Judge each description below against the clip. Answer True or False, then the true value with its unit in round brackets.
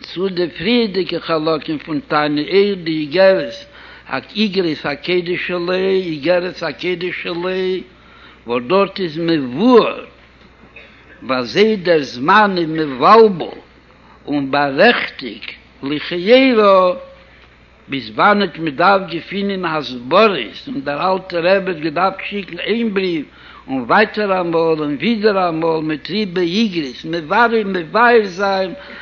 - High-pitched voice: False (180 Hz)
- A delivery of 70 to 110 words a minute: False (120 wpm)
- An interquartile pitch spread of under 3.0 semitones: False (3.9 semitones)